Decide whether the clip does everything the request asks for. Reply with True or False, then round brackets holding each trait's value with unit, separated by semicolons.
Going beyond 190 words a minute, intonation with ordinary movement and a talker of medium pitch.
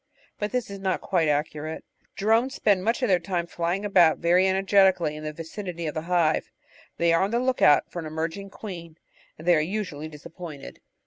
True (200 wpm; 3.7 semitones; 175 Hz)